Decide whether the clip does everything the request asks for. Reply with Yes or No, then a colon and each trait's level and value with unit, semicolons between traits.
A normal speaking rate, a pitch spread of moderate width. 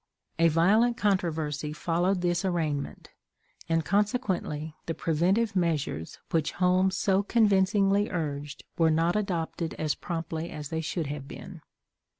No: slow, 130 wpm; average, 3.6 semitones